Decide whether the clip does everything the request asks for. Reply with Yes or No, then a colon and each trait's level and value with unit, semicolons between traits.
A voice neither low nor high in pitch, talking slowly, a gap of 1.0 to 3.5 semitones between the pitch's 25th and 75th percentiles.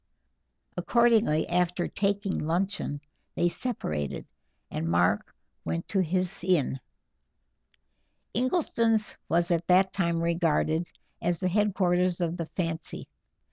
Yes: medium, 175 Hz; slow, 105 wpm; average, 3.0 semitones